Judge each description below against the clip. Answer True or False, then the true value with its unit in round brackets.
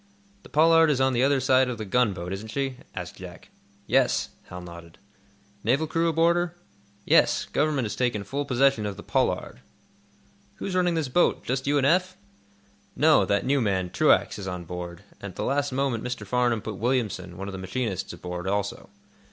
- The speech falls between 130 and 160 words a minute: False (190 wpm)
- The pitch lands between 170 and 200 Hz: False (125 Hz)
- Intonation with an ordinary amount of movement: False (6.4 semitones)